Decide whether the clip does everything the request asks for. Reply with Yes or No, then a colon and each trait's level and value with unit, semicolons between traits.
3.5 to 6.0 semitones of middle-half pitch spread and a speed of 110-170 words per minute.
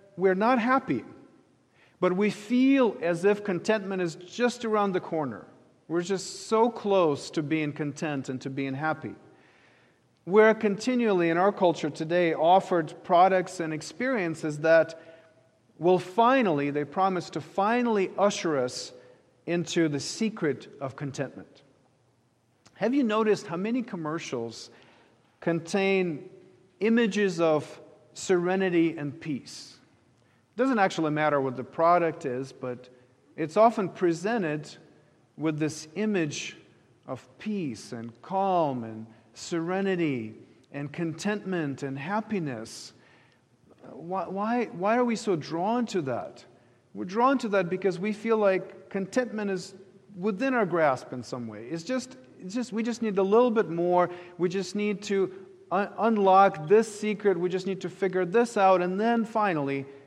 Yes: average, 5.3 semitones; average, 140 wpm